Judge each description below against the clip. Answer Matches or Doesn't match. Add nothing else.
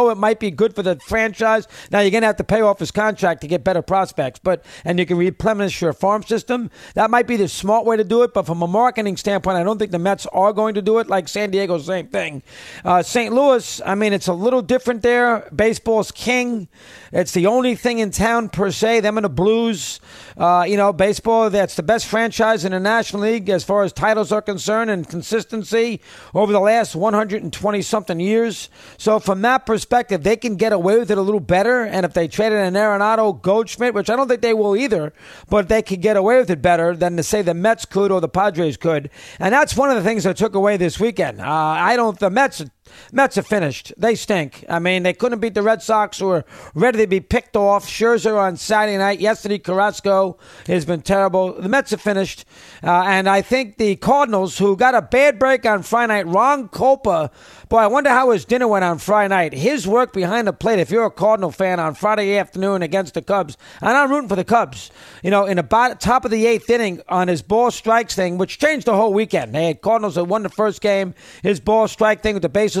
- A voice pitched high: Matches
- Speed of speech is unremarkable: Doesn't match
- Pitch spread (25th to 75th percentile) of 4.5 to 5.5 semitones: Doesn't match